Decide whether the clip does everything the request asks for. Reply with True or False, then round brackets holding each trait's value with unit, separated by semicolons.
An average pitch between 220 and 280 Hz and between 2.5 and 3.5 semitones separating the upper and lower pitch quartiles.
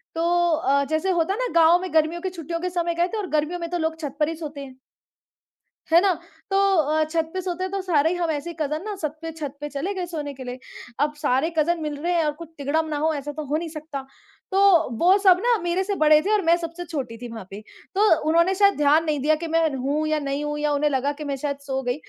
False (315 Hz; 3.0 semitones)